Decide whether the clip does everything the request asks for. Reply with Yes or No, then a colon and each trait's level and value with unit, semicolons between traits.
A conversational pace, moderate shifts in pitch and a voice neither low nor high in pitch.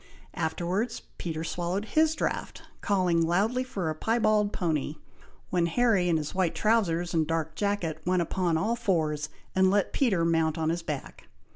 Yes: average, 160 wpm; average, 4.0 semitones; medium, 175 Hz